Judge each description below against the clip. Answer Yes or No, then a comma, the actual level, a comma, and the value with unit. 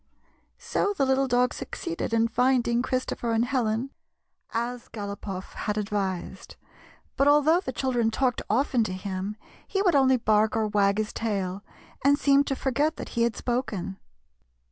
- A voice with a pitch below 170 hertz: No, high, 235 Hz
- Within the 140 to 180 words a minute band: Yes, average, 160 wpm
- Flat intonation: No, average, 4.1 semitones